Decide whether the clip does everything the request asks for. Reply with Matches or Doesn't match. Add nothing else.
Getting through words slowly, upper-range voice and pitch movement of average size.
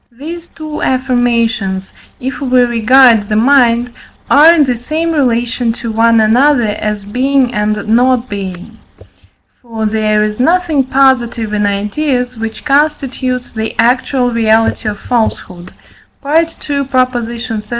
Matches